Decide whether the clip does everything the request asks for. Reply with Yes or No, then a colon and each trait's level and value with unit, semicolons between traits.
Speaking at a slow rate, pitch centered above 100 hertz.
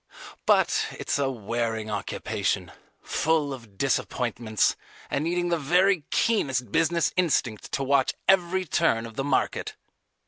Yes: slow, 130 wpm; low, 135 Hz